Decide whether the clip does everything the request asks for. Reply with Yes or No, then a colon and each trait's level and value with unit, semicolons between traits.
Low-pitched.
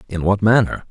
Yes: low, 100 Hz